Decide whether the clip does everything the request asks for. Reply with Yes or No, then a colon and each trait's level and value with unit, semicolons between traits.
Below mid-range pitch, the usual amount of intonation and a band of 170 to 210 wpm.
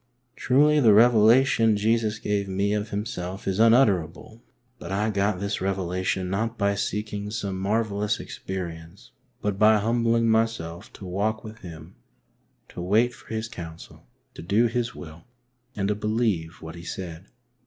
No: low, 105 Hz; average, 3.1 semitones; average, 155 wpm